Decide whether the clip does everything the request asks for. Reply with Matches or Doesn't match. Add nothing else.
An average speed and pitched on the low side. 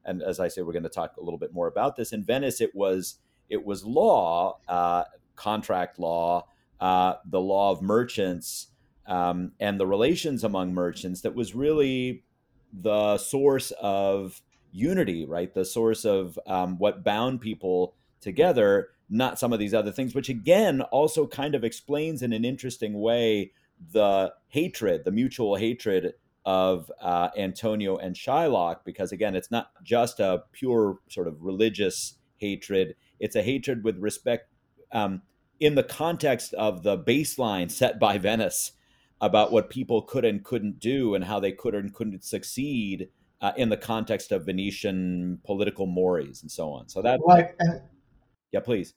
Matches